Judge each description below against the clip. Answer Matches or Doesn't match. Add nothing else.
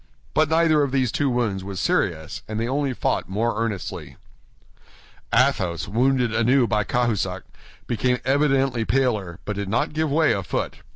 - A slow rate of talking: Doesn't match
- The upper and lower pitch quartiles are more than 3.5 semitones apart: Matches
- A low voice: Matches